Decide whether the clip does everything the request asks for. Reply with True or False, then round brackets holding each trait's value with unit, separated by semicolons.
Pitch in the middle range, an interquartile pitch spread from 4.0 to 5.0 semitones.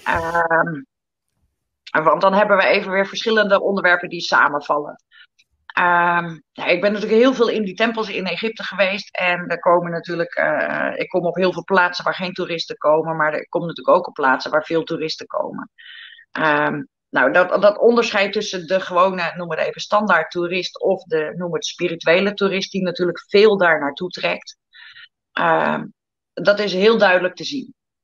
False (180 Hz; 3.3 semitones)